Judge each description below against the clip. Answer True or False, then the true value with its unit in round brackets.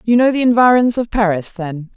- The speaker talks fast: True (215 wpm)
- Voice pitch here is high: True (215 Hz)